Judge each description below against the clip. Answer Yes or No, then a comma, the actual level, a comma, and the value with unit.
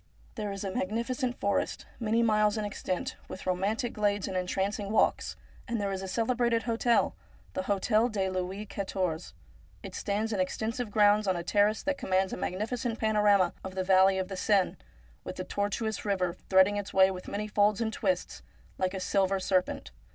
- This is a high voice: Yes, high, 205 Hz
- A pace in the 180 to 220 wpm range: Yes, average, 185 wpm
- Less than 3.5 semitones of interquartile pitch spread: Yes, narrow, 2.5 semitones